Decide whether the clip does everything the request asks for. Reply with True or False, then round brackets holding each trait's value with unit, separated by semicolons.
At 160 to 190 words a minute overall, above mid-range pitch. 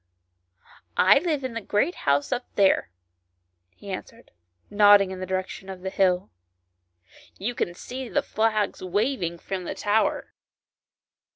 False (150 wpm; 195 Hz)